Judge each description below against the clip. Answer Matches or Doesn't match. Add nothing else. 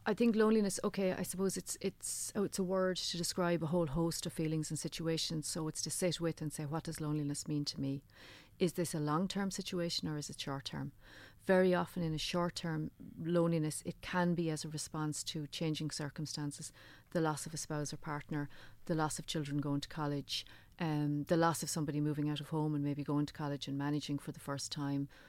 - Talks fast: Matches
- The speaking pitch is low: Doesn't match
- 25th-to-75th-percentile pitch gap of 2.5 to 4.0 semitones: Matches